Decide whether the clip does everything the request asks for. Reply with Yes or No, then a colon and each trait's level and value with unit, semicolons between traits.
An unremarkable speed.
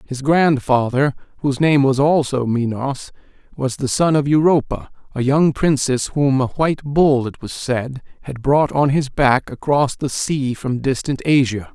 Yes: average, 170 wpm